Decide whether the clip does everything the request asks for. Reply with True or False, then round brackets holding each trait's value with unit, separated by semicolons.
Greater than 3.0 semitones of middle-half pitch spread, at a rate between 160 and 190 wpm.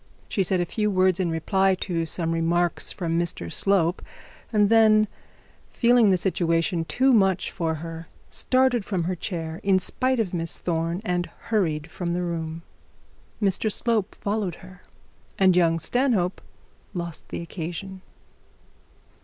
False (3.4 semitones; 145 wpm)